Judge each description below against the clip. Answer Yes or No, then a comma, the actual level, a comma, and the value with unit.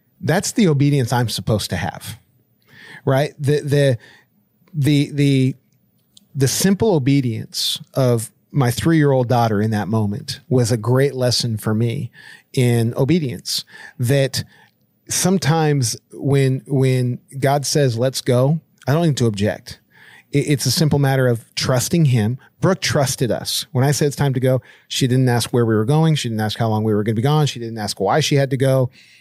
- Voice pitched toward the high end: No, low, 135 Hz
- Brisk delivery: No, average, 180 wpm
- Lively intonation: No, average, 3.2 semitones